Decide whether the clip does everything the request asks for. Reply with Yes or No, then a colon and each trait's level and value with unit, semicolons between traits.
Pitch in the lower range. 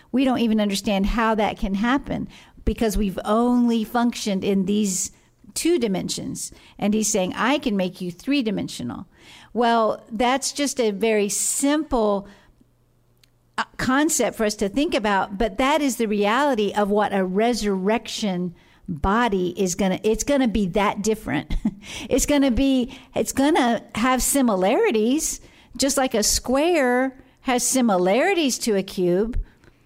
No: high, 225 Hz